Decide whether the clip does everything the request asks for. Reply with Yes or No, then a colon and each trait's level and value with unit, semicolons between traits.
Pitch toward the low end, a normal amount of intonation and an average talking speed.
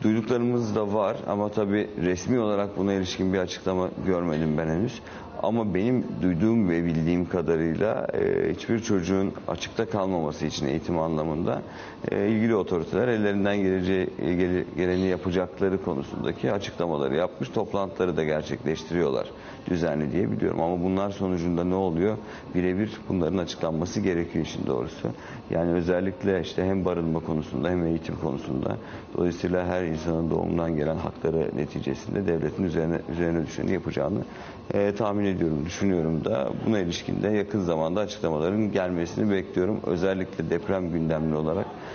Yes: very low, 90 Hz; average, 3.2 semitones; average, 130 wpm